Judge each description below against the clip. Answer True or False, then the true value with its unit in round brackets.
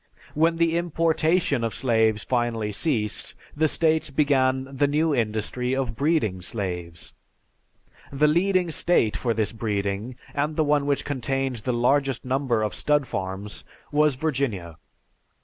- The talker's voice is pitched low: True (130 Hz)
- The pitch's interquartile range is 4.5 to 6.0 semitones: True (5.4 semitones)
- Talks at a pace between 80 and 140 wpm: True (135 wpm)